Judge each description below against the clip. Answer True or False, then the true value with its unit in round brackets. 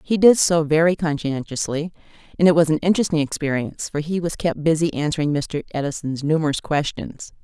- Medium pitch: True (155 Hz)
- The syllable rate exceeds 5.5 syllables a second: True (5.8 syllables/s)